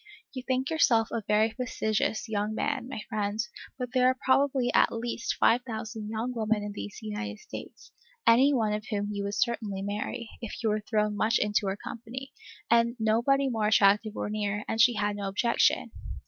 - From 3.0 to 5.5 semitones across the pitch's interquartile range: No, narrow, 2.6 semitones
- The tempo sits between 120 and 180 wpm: No, average, 190 wpm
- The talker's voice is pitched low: No, high, 220 Hz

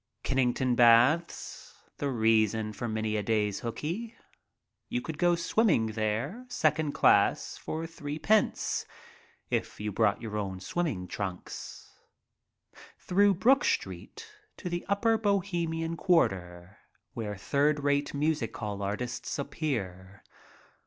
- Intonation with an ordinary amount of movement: No, wide, 8.0 semitones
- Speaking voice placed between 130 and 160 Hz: Yes, low, 135 Hz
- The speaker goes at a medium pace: No, slow, 115 wpm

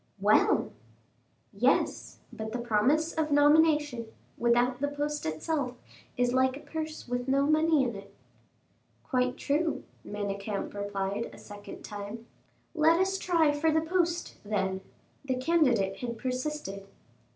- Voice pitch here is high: Yes, very high, 255 Hz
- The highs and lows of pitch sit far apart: Yes, wide, 6.3 semitones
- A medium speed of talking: No, slow, 130 wpm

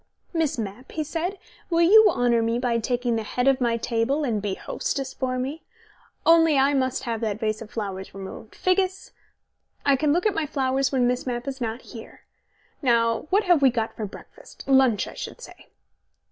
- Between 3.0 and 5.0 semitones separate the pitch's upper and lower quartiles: Yes, average, 4.2 semitones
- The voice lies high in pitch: Yes, very high, 255 Hz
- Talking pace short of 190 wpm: No, average, 195 wpm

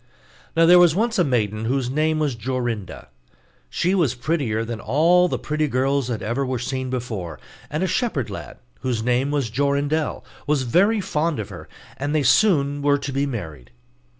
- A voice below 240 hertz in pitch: Yes, medium, 140 Hz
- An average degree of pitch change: Yes, average, 4.4 semitones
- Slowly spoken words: No, average, 180 wpm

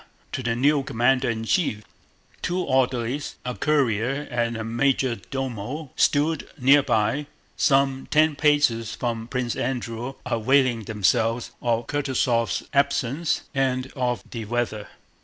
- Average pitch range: Yes, average, 3.2 semitones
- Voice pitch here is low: Yes, low, 125 Hz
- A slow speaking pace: Yes, slow, 130 wpm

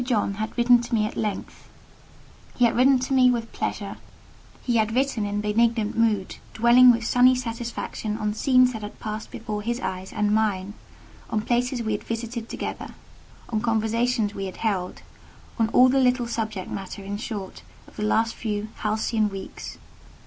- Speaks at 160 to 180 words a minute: Yes, average, 165 wpm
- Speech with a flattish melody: Yes, narrow, 2.3 semitones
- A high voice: Yes, high, 225 Hz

